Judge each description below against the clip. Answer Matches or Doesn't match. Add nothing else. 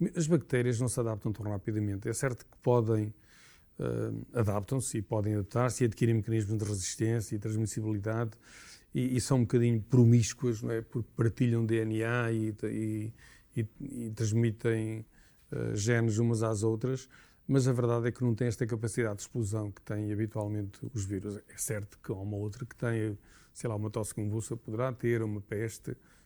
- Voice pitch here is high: Doesn't match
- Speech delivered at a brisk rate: Doesn't match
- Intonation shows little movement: Matches